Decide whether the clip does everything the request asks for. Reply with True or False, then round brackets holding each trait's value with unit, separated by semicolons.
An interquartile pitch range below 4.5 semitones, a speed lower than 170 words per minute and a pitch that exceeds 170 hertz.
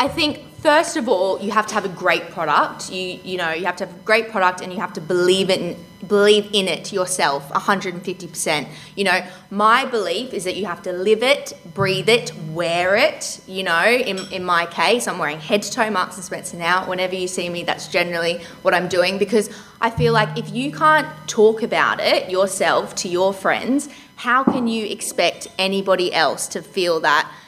False (3.3 semitones; 205 wpm; 190 Hz)